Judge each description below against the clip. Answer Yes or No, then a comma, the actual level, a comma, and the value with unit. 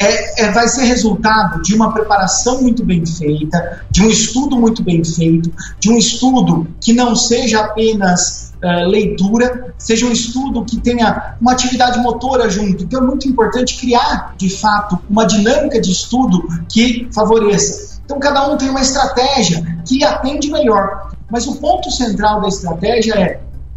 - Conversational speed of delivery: Yes, average, 160 wpm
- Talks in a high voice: Yes, high, 220 Hz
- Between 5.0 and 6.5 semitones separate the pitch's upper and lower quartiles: No, average, 4.0 semitones